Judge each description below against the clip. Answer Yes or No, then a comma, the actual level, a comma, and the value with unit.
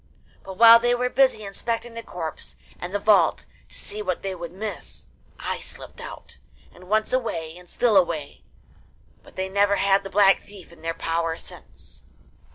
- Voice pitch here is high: Yes, high, 195 Hz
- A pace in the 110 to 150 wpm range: No, average, 175 wpm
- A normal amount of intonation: Yes, average, 3.9 semitones